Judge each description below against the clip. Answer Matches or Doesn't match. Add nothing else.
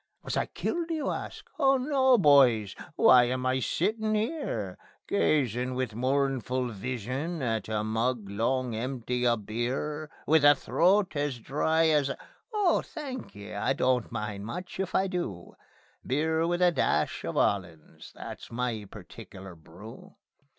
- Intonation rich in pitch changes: Matches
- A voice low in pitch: Matches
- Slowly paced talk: Doesn't match